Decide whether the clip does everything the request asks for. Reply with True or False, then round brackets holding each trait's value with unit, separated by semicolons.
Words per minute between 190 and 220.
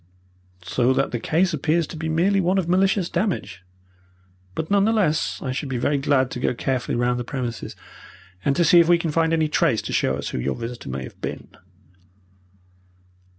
True (200 wpm)